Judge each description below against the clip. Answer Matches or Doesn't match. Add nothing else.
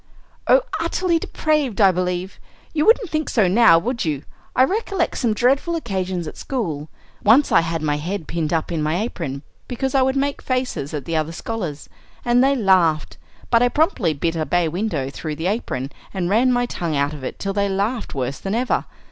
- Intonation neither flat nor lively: Doesn't match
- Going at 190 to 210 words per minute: Matches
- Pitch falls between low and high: Doesn't match